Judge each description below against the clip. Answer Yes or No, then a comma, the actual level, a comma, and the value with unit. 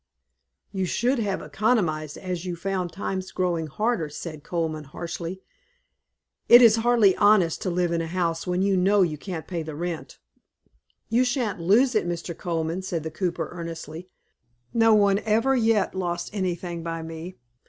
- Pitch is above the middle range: No, medium, 180 Hz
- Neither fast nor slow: Yes, average, 165 wpm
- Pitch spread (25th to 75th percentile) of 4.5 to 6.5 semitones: No, average, 3.6 semitones